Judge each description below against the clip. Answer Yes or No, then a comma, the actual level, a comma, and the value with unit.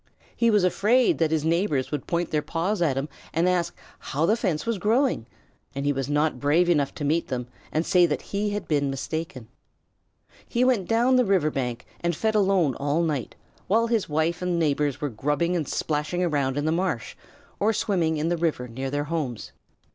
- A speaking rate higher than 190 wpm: Yes, average, 200 wpm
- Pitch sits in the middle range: Yes, medium, 160 Hz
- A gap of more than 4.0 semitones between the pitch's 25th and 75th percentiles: Yes, average, 4.4 semitones